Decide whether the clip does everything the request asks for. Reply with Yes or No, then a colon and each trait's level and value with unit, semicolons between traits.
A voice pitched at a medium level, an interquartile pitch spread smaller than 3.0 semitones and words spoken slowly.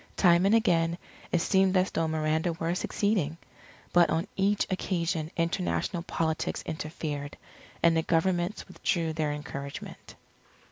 Yes: medium, 170 Hz; narrow, 2.6 semitones; slow, 130 wpm